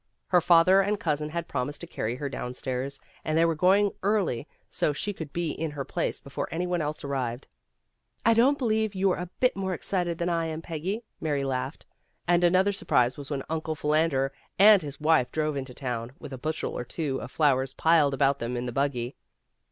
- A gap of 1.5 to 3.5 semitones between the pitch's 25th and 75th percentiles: No, average, 4.6 semitones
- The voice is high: No, medium, 155 Hz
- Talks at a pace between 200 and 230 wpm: Yes, fast, 205 wpm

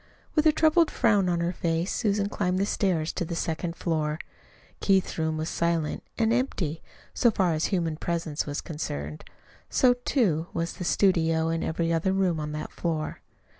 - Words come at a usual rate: Yes, average, 175 wpm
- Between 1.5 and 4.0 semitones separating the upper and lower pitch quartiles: Yes, average, 3.5 semitones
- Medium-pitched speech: Yes, medium, 170 Hz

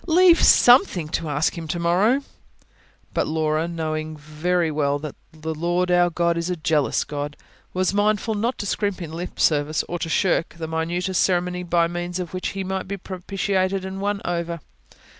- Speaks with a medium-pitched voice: Yes, medium, 175 Hz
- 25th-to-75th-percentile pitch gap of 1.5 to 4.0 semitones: Yes, average, 2.9 semitones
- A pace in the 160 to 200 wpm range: Yes, average, 180 wpm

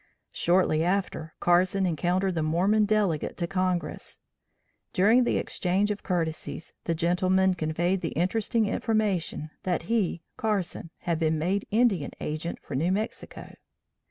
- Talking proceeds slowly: Yes, slow, 130 wpm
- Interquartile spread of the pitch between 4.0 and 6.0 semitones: No, average, 3.1 semitones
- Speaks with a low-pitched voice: No, medium, 180 Hz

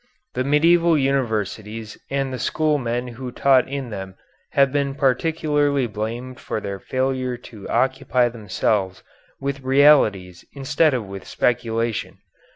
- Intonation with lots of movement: No, average, 3.7 semitones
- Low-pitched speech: Yes, low, 130 Hz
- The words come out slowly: Yes, slow, 130 wpm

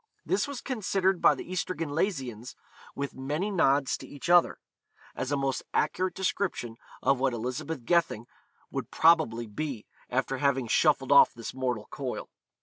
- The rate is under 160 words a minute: Yes, average, 145 wpm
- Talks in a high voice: No, medium, 140 Hz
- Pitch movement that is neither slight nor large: No, wide, 5.7 semitones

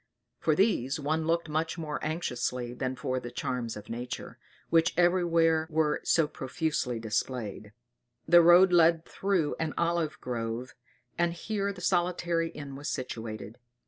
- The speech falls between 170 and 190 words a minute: No, average, 145 wpm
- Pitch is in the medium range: Yes, medium, 155 Hz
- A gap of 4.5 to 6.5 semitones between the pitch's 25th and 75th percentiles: Yes, average, 5.3 semitones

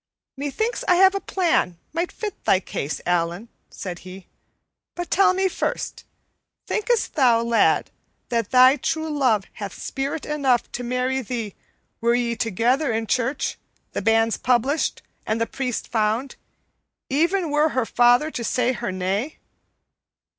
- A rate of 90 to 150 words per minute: Yes, average, 145 wpm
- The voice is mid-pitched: No, very high, 250 Hz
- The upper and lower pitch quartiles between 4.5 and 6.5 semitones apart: Yes, average, 5.1 semitones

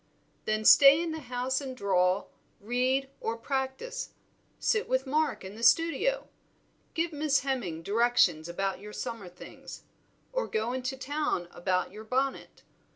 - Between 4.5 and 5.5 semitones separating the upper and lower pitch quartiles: Yes, average, 5.2 semitones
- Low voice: No, very high, 255 Hz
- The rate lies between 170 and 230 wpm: No, average, 145 wpm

